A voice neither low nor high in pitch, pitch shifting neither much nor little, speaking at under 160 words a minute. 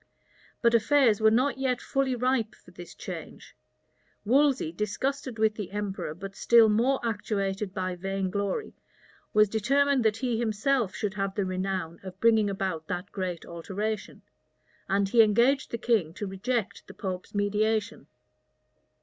No: high, 210 Hz; average, 3.5 semitones; average, 150 wpm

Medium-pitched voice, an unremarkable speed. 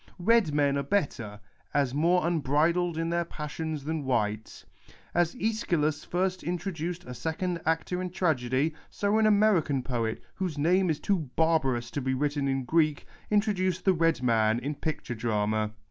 Yes: medium, 155 Hz; average, 160 wpm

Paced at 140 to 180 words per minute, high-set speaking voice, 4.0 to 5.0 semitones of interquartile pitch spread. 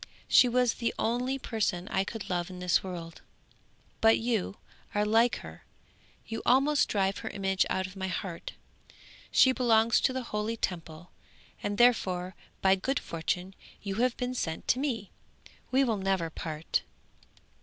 Yes: average, 155 wpm; high, 205 Hz; average, 4.7 semitones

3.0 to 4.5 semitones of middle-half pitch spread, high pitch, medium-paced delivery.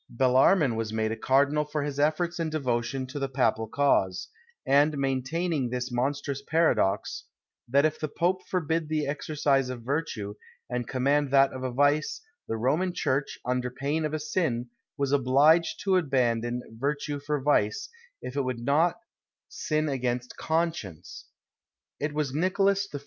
No: average, 3.5 semitones; medium, 140 Hz; average, 155 wpm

